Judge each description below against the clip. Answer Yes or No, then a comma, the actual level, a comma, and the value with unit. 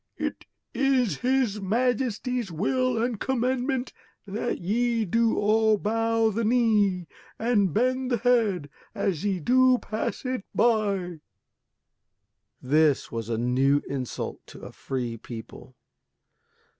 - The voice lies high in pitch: Yes, high, 220 Hz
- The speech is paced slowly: Yes, slow, 120 wpm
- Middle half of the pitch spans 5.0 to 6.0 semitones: Yes, average, 5.3 semitones